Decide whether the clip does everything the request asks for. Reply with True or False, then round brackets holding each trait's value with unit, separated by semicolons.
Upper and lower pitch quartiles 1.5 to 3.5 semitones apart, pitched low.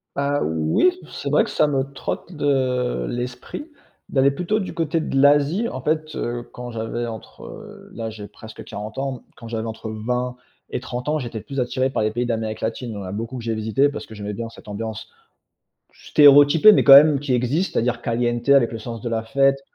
False (3.9 semitones; 125 Hz)